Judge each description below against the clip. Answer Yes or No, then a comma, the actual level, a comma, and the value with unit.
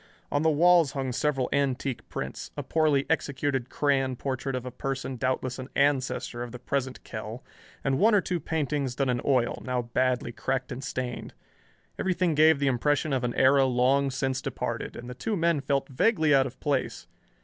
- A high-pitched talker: No, low, 135 Hz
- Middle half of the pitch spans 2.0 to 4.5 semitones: Yes, narrow, 2.4 semitones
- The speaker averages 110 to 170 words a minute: No, average, 185 wpm